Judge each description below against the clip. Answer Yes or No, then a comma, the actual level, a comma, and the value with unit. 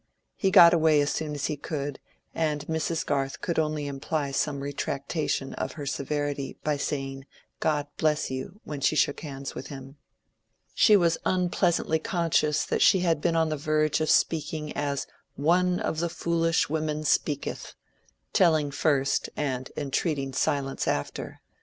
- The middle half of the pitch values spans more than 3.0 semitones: No, narrow, 2.5 semitones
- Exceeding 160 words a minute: No, average, 155 wpm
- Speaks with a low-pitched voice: No, medium, 150 Hz